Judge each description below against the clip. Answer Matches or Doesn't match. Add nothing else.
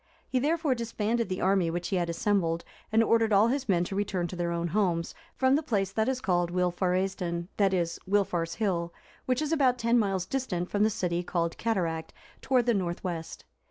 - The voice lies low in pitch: Doesn't match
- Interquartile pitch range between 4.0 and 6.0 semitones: Matches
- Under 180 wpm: Doesn't match